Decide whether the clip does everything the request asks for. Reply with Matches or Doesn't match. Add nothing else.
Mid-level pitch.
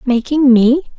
Doesn't match